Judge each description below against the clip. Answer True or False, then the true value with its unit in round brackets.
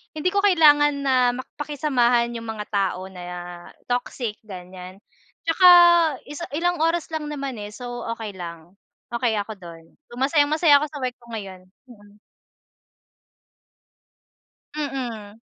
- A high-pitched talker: True (245 Hz)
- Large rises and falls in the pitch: True (6.2 semitones)